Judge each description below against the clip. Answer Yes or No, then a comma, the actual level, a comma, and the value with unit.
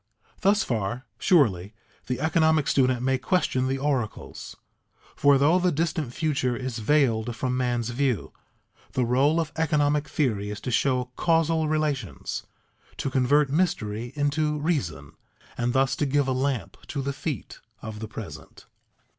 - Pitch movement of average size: Yes, average, 3.9 semitones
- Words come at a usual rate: Yes, average, 145 wpm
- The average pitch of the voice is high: No, low, 135 Hz